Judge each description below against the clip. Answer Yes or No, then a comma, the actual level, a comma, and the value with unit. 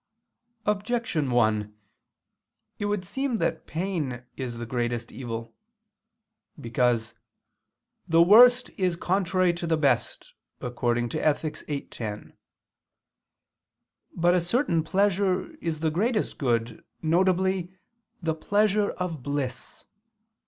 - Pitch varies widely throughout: Yes, wide, 7.7 semitones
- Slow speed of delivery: Yes, slow, 105 wpm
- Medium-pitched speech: Yes, medium, 165 Hz